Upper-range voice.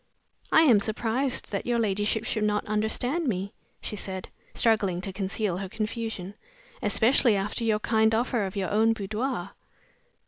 Yes: high, 215 Hz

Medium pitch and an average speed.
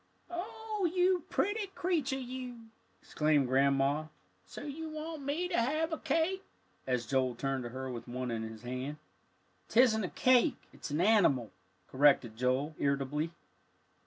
Yes: medium, 180 Hz; average, 145 wpm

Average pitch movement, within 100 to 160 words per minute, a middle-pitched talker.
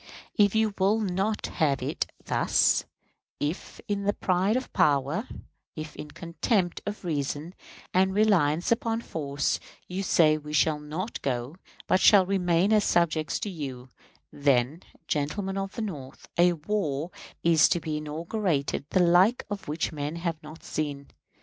Yes: average, 4.7 semitones; average, 150 wpm; medium, 170 Hz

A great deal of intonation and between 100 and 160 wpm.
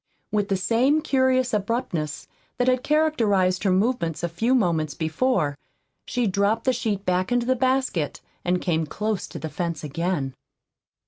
Yes: wide, 6.6 semitones; average, 155 wpm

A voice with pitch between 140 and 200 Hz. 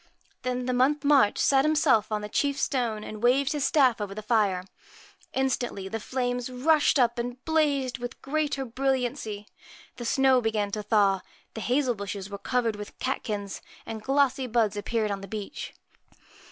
No: high, 245 Hz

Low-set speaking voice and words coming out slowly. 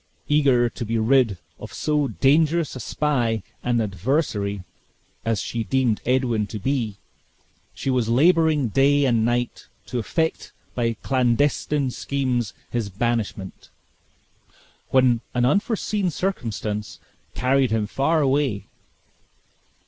Yes: low, 125 Hz; slow, 115 wpm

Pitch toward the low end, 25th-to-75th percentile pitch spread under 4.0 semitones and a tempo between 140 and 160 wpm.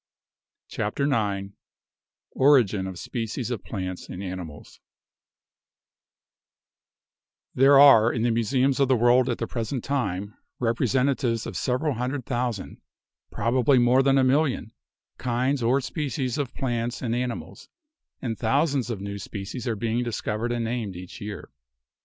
Yes: low, 120 Hz; average, 3.2 semitones; average, 145 wpm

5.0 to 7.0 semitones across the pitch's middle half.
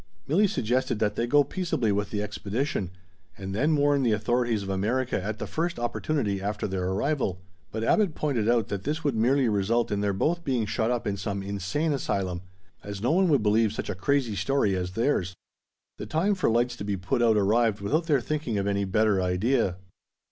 Yes: wide, 5.5 semitones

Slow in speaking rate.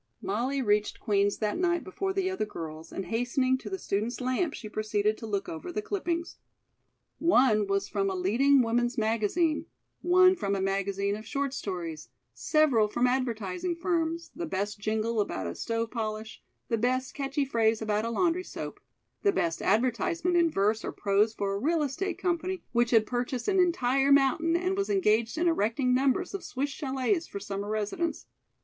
No: average, 180 wpm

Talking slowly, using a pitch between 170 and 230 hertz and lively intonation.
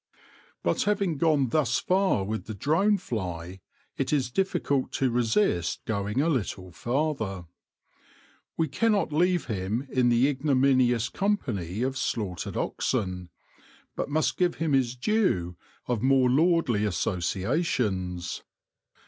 No: slow, 125 wpm; low, 125 Hz; wide, 7.5 semitones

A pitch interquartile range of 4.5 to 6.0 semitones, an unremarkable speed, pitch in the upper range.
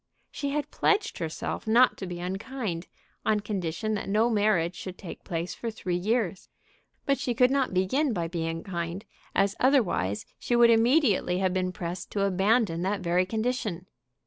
Yes: average, 4.8 semitones; average, 170 wpm; high, 195 Hz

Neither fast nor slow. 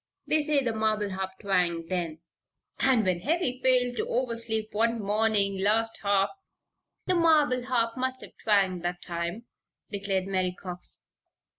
Yes: average, 145 wpm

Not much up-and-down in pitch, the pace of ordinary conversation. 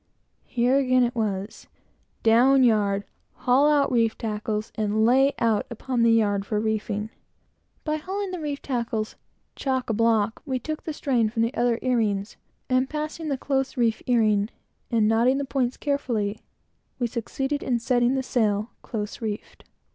No: average, 3.5 semitones; average, 160 wpm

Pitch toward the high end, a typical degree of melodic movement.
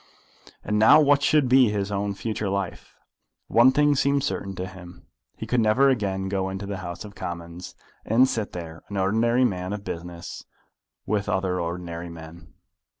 No: low, 100 Hz; average, 4.4 semitones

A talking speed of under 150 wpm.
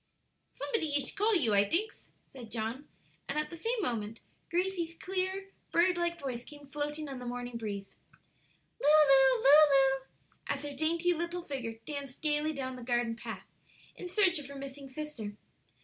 No: average, 165 wpm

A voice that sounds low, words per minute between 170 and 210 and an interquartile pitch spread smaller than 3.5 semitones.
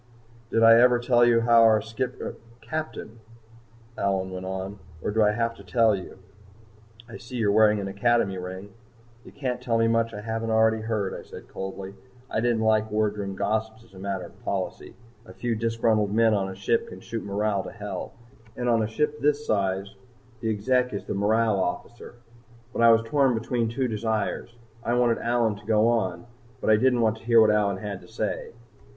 Yes: low, 110 Hz; average, 200 wpm; narrow, 2.4 semitones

